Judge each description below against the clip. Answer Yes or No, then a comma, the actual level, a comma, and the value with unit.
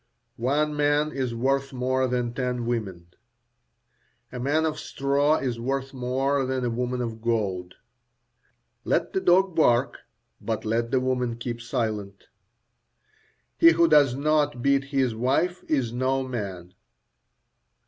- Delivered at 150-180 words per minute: No, slow, 135 wpm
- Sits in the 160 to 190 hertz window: No, low, 130 Hz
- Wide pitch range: No, average, 3.0 semitones